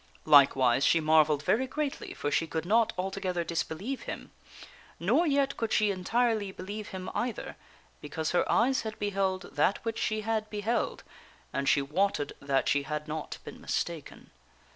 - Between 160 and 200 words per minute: Yes, average, 165 wpm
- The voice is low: No, high, 190 Hz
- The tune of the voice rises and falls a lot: Yes, wide, 6.0 semitones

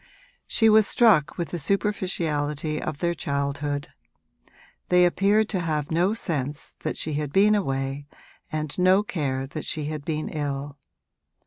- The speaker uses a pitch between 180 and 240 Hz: No, medium, 155 Hz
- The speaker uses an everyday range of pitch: Yes, average, 4.3 semitones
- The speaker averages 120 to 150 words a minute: Yes, average, 145 wpm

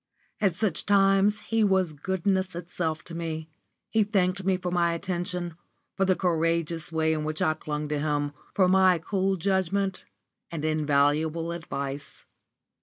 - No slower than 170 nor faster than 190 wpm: No, average, 150 wpm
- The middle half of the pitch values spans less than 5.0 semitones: Yes, average, 3.3 semitones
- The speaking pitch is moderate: Yes, medium, 170 Hz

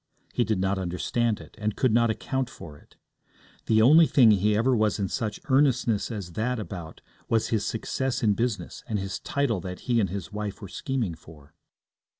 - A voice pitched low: Yes, low, 110 Hz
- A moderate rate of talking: Yes, average, 190 wpm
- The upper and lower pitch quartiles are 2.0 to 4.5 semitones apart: Yes, average, 3.7 semitones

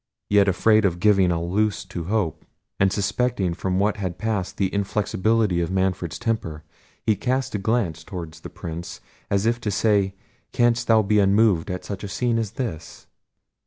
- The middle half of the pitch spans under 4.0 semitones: Yes, average, 3.2 semitones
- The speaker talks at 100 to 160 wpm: No, average, 175 wpm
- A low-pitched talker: Yes, low, 100 Hz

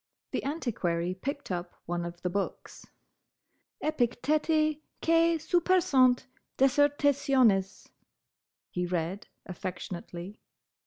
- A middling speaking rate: No, slow, 85 wpm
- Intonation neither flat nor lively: No, wide, 8.7 semitones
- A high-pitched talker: Yes, high, 245 Hz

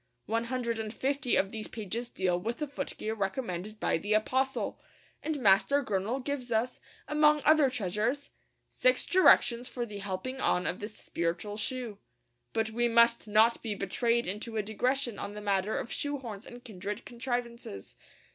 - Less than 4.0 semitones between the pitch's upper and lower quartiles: Yes, average, 3.6 semitones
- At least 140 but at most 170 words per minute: Yes, average, 165 wpm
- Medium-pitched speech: No, high, 230 Hz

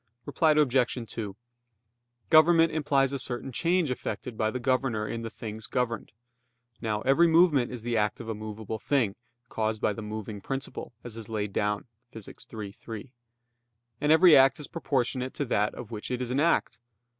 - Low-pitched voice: Yes, low, 120 Hz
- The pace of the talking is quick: No, average, 180 wpm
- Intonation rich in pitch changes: No, average, 4.2 semitones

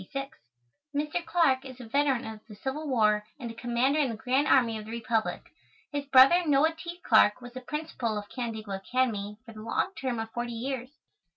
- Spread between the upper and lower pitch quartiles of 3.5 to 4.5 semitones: Yes, average, 3.8 semitones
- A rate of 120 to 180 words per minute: No, average, 195 wpm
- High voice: Yes, very high, 250 Hz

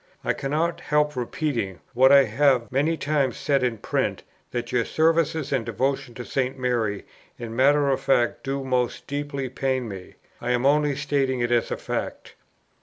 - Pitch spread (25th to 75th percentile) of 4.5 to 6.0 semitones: No, average, 2.9 semitones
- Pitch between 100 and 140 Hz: Yes, low, 135 Hz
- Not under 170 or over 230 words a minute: Yes, average, 175 wpm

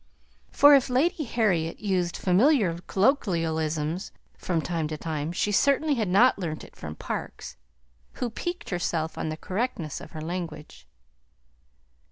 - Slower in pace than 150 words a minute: Yes, average, 140 wpm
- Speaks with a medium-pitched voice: Yes, medium, 180 Hz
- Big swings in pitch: Yes, wide, 7.1 semitones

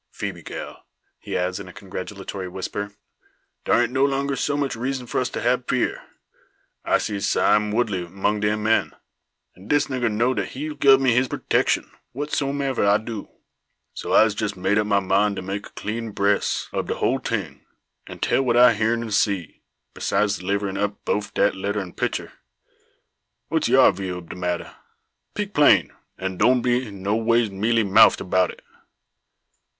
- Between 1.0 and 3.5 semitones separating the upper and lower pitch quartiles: No, average, 3.9 semitones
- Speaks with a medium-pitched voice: No, low, 105 Hz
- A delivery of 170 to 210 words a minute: Yes, average, 175 wpm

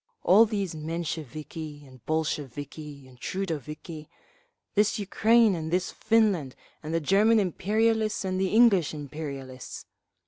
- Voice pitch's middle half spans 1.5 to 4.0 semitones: No, wide, 5.5 semitones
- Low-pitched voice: No, medium, 165 Hz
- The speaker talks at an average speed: No, slow, 115 wpm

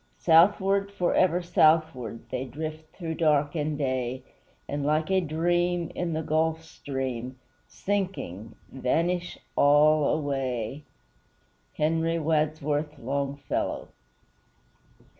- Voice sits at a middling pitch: Yes, medium, 155 Hz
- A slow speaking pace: Yes, slow, 95 wpm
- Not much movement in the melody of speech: No, average, 3.1 semitones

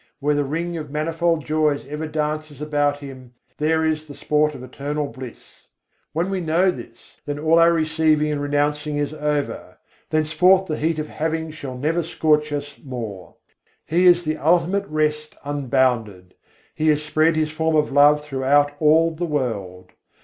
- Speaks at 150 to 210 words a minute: Yes, average, 165 wpm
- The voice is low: No, medium, 150 Hz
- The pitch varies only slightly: Yes, narrow, 1.8 semitones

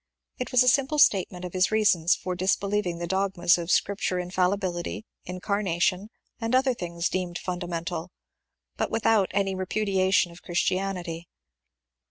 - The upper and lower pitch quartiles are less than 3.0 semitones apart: Yes, narrow, 2.6 semitones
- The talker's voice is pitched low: No, medium, 185 Hz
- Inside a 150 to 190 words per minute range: No, average, 140 wpm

